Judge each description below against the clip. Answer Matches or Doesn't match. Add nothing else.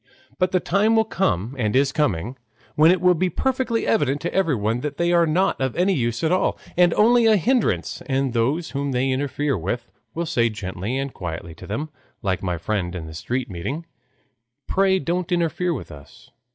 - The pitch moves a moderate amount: Doesn't match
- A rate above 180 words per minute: Matches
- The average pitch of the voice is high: Doesn't match